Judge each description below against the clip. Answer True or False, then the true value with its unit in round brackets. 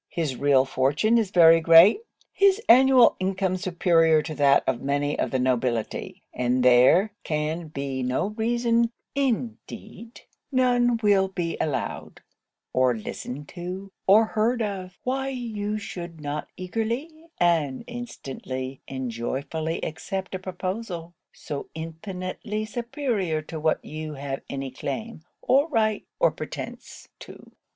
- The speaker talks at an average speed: False (130 wpm)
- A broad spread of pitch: True (7.5 semitones)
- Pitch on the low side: False (180 Hz)